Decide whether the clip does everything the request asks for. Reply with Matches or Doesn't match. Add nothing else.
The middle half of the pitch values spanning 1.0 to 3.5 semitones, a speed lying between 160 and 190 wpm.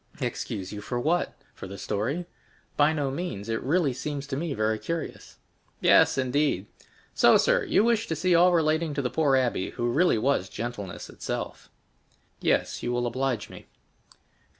Doesn't match